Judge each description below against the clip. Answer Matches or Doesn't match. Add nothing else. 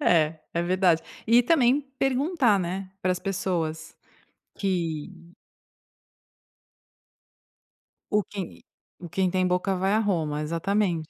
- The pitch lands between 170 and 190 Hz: Matches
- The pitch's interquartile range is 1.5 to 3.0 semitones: Doesn't match